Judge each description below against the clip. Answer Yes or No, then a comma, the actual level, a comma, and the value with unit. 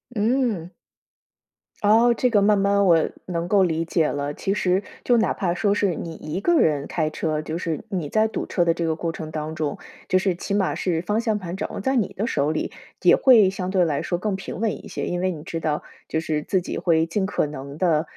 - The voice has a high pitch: No, medium, 180 Hz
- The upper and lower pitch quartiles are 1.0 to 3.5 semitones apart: No, average, 4.2 semitones